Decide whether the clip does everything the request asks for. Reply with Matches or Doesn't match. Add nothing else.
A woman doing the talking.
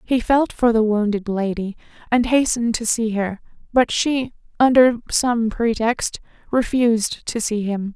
Matches